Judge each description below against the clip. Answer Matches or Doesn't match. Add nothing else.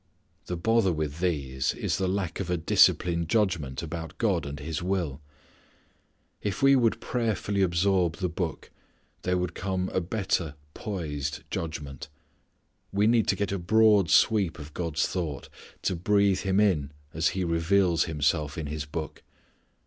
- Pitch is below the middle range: Matches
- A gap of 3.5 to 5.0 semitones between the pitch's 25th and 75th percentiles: Matches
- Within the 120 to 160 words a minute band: Matches